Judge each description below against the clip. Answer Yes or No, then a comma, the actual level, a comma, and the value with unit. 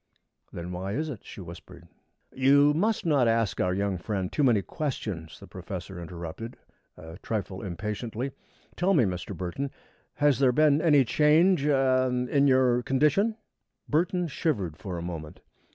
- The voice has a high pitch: No, low, 125 Hz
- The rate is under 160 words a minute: Yes, average, 150 wpm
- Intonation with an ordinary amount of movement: No, wide, 7.9 semitones